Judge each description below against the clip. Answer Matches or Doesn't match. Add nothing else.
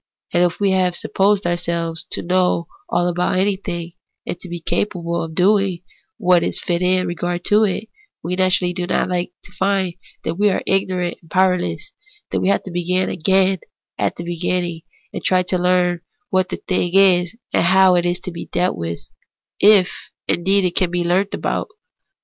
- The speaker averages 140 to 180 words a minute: Doesn't match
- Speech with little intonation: Matches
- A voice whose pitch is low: Doesn't match